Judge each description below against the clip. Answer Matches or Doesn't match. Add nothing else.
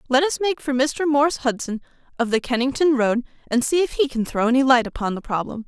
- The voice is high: Matches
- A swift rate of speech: Matches